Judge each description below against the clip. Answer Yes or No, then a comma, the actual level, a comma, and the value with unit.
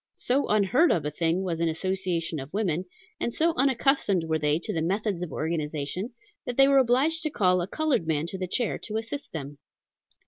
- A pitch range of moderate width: No, wide, 7.2 semitones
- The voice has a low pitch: No, medium, 185 Hz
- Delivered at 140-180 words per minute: No, fast, 205 wpm